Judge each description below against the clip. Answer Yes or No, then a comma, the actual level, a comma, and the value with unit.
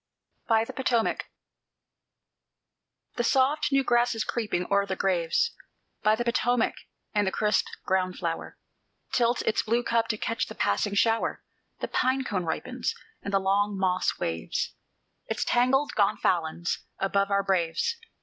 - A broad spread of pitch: No, average, 4.1 semitones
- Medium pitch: No, high, 210 Hz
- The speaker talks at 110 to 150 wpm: Yes, average, 145 wpm